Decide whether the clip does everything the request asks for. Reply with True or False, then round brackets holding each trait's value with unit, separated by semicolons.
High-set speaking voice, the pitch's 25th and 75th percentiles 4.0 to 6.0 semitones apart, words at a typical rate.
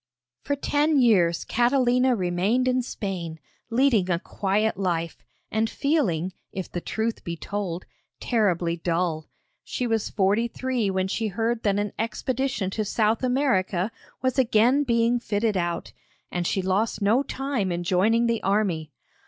True (215 Hz; 4.7 semitones; 145 wpm)